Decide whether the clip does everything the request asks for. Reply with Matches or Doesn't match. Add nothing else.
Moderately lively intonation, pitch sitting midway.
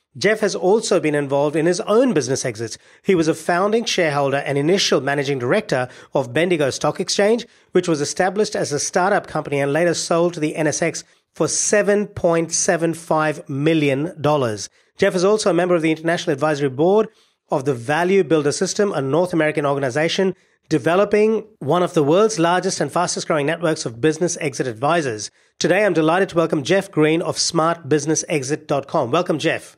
Matches